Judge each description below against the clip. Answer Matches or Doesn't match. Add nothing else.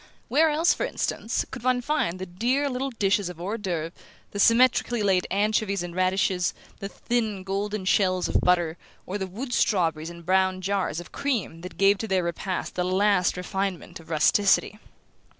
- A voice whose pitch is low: Doesn't match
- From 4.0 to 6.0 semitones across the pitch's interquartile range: Doesn't match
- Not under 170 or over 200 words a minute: Matches